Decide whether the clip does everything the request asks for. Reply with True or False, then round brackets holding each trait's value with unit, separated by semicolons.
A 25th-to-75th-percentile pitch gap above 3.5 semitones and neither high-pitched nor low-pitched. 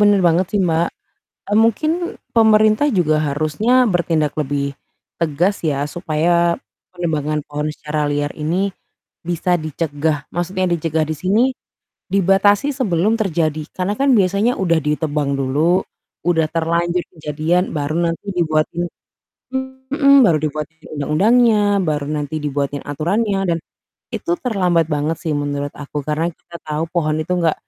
True (4.2 semitones; 165 Hz)